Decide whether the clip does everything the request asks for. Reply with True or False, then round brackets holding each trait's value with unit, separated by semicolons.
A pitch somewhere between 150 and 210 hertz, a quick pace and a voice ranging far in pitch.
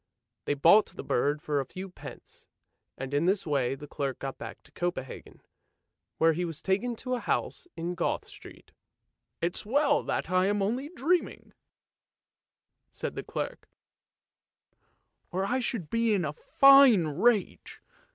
False (185 Hz; 155 wpm; 7.7 semitones)